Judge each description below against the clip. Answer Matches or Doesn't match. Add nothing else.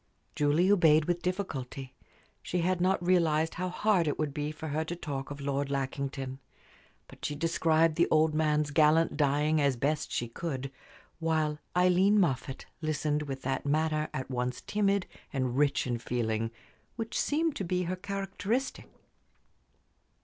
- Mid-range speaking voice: Matches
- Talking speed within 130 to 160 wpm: Matches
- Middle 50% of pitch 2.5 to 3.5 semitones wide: Doesn't match